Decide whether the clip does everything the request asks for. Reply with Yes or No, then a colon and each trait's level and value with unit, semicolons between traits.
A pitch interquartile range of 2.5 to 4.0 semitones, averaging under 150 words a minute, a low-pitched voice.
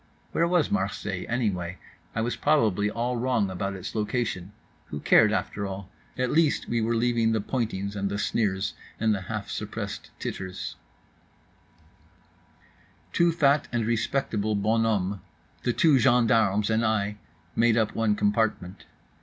Yes: average, 3.1 semitones; average, 140 wpm; low, 110 Hz